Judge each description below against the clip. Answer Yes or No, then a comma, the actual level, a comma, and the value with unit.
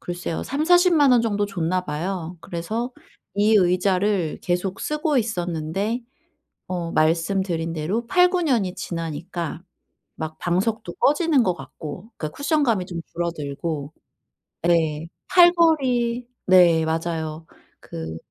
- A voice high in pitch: No, medium, 180 Hz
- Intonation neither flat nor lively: No, wide, 6.1 semitones